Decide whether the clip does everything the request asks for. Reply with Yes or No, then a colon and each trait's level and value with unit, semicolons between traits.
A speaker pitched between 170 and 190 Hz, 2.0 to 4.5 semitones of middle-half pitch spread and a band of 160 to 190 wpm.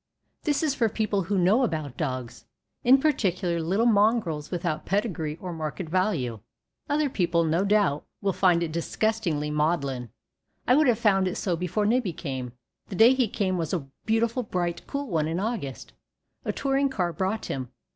No: medium, 185 Hz; wide, 5.6 semitones; average, 175 wpm